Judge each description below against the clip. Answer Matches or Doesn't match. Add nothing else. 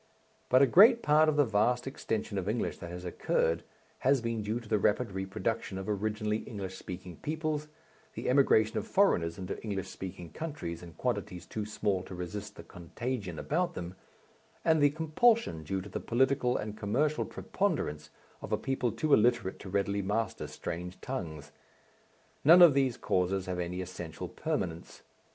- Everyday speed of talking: Matches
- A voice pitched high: Doesn't match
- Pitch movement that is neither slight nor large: Doesn't match